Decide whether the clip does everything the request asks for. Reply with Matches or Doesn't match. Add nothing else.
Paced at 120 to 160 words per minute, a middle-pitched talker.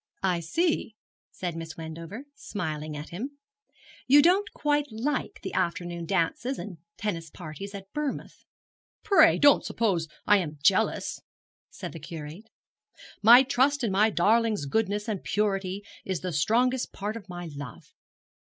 Doesn't match